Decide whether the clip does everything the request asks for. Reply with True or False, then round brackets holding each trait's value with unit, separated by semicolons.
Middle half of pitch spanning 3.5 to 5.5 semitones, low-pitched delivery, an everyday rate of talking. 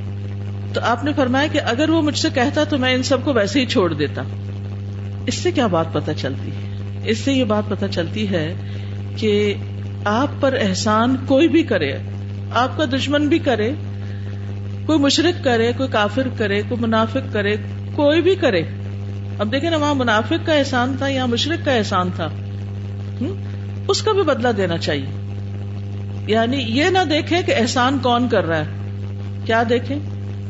True (4.4 semitones; 100 Hz; 175 wpm)